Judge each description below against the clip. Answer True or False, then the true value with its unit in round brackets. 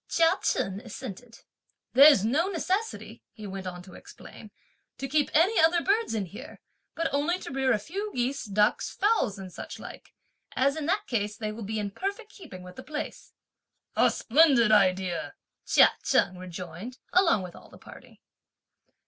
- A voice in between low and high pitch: False (245 Hz)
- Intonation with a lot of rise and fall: True (8.5 semitones)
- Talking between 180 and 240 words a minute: False (170 wpm)